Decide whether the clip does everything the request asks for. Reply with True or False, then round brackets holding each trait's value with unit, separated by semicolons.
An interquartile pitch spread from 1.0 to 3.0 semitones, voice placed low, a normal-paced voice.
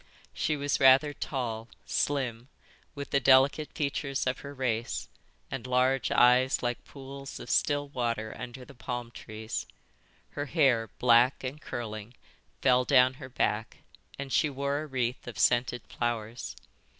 True (2.7 semitones; 130 Hz; 145 wpm)